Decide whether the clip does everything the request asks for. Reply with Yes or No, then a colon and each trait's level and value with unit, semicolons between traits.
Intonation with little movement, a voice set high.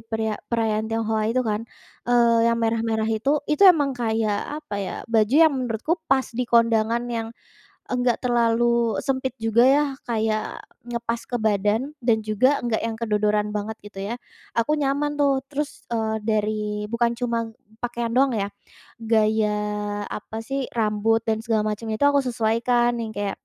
Yes: narrow, 1.8 semitones; high, 230 Hz